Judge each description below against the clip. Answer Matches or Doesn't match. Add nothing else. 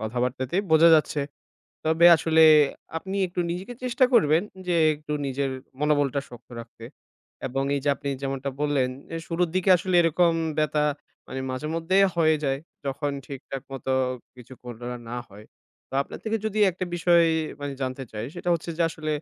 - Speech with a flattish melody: Doesn't match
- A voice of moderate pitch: Matches